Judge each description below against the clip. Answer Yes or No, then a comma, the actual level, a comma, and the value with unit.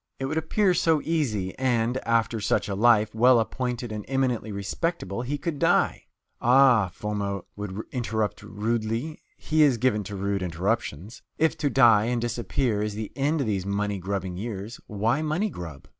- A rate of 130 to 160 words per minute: No, average, 170 wpm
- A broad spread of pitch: No, average, 4.5 semitones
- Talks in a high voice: No, low, 115 Hz